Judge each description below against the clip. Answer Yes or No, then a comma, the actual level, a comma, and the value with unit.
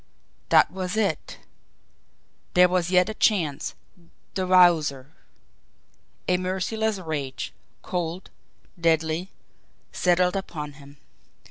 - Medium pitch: Yes, medium, 180 Hz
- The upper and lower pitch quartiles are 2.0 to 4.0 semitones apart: Yes, average, 2.8 semitones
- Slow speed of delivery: Yes, slow, 95 wpm